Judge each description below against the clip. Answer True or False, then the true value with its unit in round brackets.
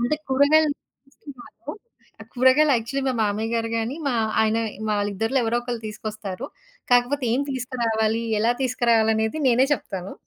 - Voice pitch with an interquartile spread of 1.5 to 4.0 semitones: True (3.0 semitones)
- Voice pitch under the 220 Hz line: False (235 Hz)